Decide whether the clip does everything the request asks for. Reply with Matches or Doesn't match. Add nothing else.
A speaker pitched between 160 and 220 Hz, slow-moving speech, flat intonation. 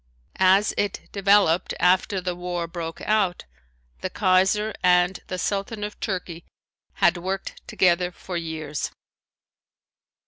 Matches